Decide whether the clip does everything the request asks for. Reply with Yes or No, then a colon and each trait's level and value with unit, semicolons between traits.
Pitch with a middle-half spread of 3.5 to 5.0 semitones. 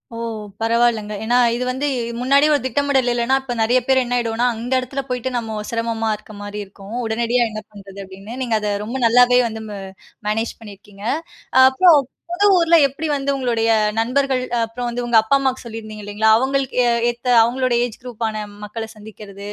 No: average, 2.8 semitones